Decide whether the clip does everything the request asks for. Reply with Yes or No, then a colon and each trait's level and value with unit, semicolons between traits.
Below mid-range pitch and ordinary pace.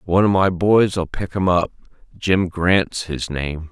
Yes: very low, 90 Hz; average, 180 wpm